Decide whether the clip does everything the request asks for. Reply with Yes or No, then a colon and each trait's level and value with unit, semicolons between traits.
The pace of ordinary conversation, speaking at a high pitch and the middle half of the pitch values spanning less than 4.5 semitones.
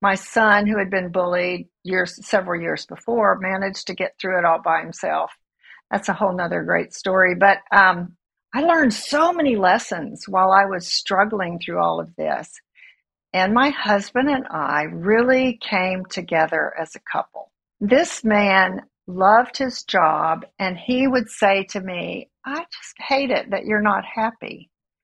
Yes: average, 165 wpm; high, 195 Hz; average, 3.9 semitones